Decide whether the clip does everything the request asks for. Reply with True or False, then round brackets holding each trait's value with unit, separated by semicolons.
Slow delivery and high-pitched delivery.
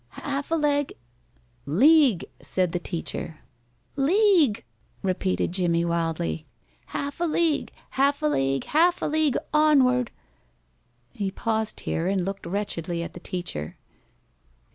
True (125 wpm; 210 Hz)